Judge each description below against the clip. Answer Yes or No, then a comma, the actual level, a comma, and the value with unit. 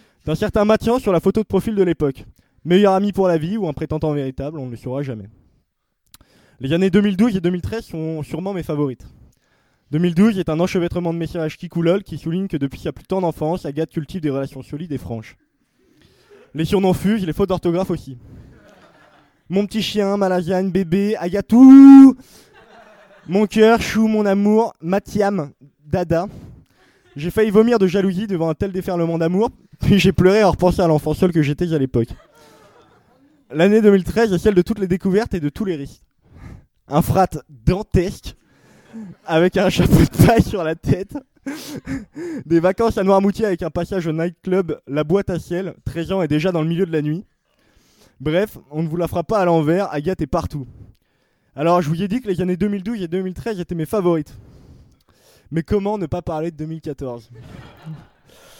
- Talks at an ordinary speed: Yes, average, 185 wpm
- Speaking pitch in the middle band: Yes, medium, 175 Hz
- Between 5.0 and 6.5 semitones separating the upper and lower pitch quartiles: No, average, 4.4 semitones